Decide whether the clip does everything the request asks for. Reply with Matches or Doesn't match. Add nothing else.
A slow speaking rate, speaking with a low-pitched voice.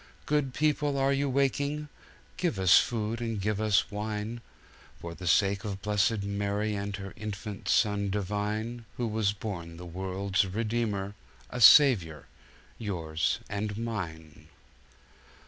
Matches